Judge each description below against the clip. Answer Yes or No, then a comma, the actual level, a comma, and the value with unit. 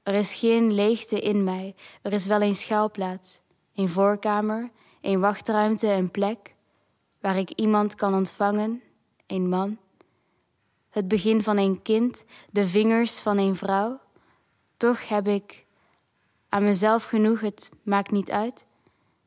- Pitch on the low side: No, high, 205 Hz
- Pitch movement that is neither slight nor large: No, narrow, 1.8 semitones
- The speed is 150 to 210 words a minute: No, slow, 135 wpm